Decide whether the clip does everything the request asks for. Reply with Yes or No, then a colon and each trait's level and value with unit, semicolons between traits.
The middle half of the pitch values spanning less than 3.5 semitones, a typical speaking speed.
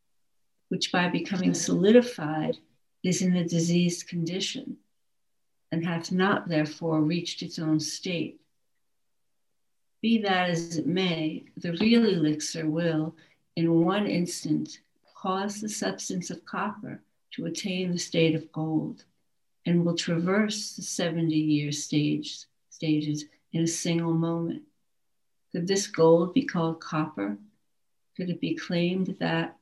No: average, 2.9 semitones; slow, 125 wpm